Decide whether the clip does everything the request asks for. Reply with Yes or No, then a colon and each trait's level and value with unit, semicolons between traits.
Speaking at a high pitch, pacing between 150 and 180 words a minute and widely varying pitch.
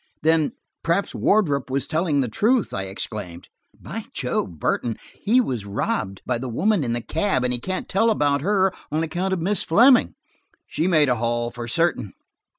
No: medium, 150 Hz; average, 175 wpm; wide, 8.0 semitones